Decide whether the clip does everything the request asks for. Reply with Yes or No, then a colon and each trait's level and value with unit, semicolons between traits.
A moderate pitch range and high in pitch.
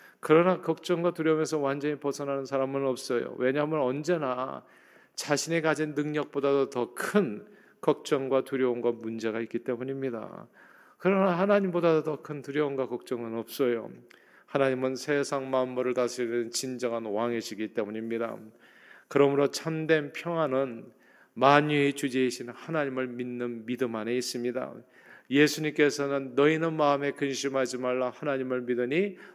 No: average, 3.2 semitones; low, 135 Hz